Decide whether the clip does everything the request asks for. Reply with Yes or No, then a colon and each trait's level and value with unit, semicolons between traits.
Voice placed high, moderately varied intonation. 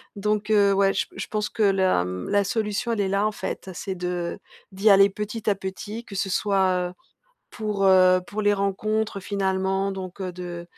No: high, 195 Hz; narrow, 1.9 semitones